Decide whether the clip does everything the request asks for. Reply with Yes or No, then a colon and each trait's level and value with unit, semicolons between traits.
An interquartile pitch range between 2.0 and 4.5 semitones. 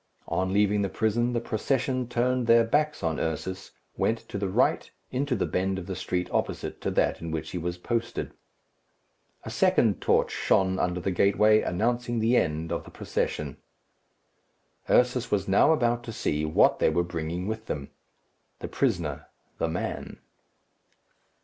No: average, 5.2 semitones